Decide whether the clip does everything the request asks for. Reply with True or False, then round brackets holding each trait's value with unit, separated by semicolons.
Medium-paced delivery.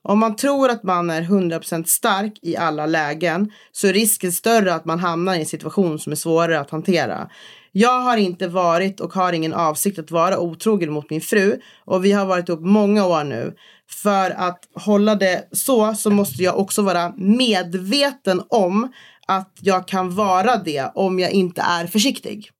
True (185 wpm)